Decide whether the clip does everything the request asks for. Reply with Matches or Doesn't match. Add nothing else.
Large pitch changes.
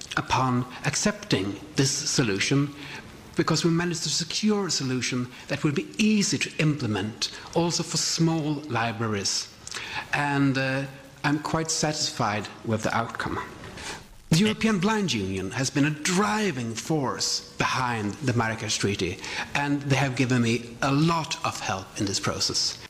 Matches